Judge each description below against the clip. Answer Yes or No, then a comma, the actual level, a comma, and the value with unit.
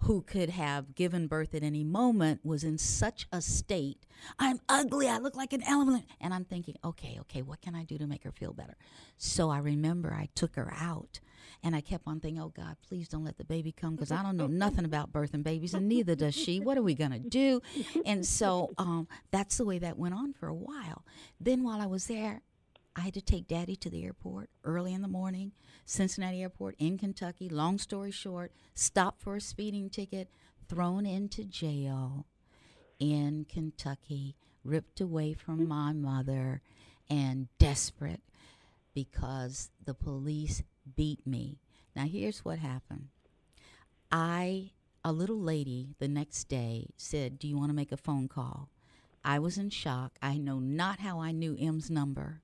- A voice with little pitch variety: No, average, 4.9 semitones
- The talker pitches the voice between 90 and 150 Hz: No, medium, 160 Hz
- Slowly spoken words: No, average, 185 wpm